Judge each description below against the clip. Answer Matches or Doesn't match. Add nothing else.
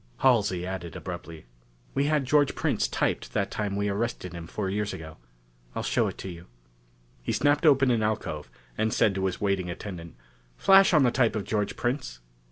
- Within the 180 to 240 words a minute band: Matches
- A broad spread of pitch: Matches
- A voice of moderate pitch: Doesn't match